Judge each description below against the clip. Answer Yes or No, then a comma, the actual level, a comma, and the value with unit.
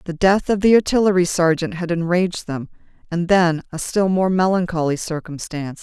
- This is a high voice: No, medium, 175 Hz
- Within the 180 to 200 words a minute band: No, average, 165 wpm